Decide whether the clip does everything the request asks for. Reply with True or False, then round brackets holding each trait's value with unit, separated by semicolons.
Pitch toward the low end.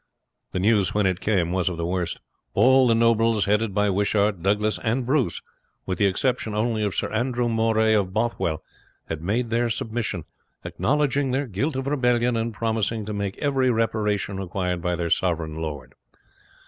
True (110 Hz)